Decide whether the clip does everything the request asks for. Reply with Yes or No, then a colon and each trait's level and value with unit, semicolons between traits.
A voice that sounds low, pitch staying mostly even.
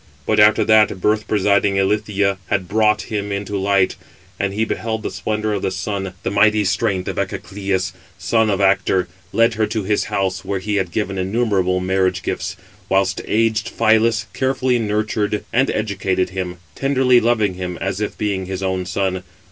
Yes: low, 100 Hz; narrow, 2.3 semitones